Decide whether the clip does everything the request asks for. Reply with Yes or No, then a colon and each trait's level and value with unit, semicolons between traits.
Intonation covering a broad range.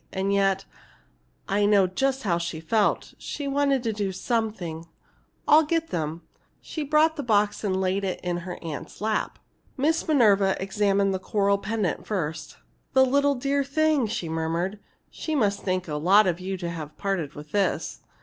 Yes: wide, 5.8 semitones